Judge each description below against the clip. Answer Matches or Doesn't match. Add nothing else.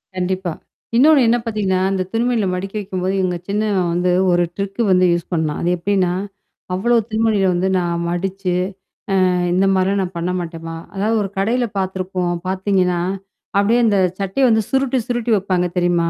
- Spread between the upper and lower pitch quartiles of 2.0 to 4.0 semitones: Matches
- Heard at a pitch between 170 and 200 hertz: Matches